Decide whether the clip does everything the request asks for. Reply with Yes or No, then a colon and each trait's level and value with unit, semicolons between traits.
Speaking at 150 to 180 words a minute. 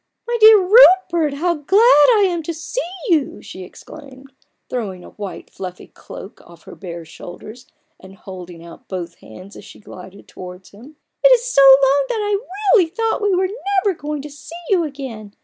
No: average, 195 wpm